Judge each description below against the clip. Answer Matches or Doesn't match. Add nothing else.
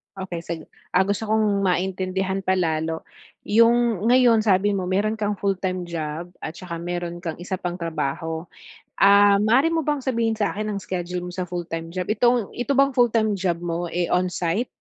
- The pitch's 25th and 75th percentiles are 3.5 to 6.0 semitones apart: Matches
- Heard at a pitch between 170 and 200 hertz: Matches